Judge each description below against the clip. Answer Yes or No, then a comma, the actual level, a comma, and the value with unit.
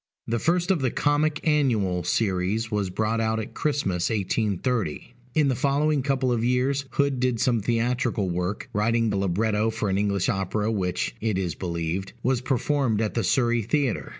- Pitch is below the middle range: Yes, low, 115 Hz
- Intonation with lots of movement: No, average, 4.7 semitones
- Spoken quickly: No, average, 175 wpm